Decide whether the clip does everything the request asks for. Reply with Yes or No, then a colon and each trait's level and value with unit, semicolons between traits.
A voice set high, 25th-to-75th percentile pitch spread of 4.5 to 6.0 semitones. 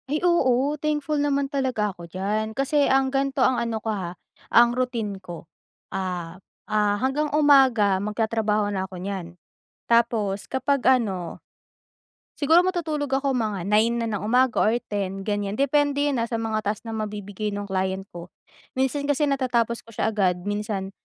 Yes: high, 225 Hz; average, 5.0 semitones